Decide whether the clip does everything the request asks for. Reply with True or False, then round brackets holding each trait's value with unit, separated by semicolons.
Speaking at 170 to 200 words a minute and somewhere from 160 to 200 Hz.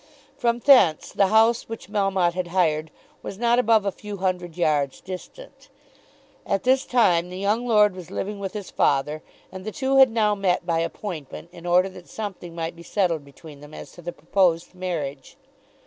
True (185 wpm; 185 Hz)